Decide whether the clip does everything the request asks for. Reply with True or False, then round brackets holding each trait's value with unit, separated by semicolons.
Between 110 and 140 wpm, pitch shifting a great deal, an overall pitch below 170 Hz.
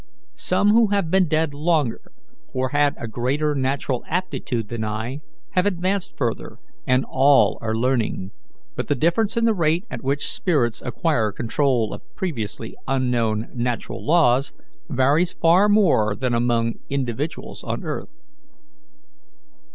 True (135 wpm; 6.1 semitones; 135 Hz)